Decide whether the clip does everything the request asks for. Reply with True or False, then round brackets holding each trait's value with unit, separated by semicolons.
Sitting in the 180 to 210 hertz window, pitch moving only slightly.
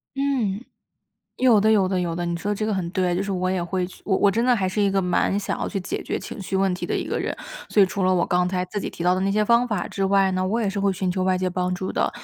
True (190 Hz; 2.0 semitones)